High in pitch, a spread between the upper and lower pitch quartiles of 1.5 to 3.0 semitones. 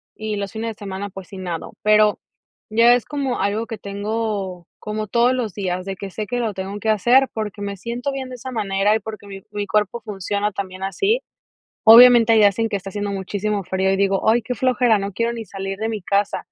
Yes: high, 210 Hz; average, 2.7 semitones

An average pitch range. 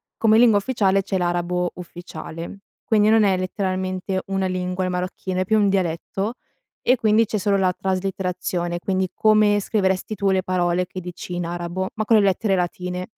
No: narrow, 2.2 semitones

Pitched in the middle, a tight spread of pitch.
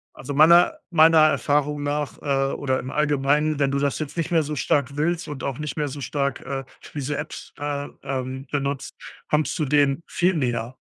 Yes: medium, 145 Hz; narrow, 1.7 semitones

